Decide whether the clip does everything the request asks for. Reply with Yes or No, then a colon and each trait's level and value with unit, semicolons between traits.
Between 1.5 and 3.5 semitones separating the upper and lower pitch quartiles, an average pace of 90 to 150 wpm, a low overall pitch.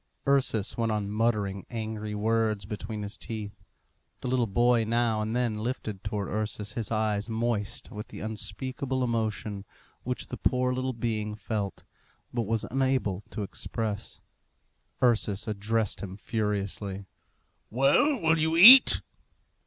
Yes: average, 2.7 semitones; slow, 135 wpm; low, 110 Hz